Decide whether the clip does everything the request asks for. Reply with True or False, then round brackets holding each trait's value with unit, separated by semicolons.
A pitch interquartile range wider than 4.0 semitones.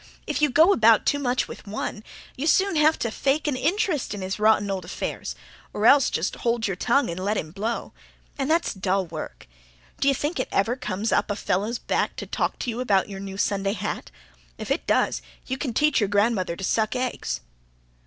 True (5.6 semitones)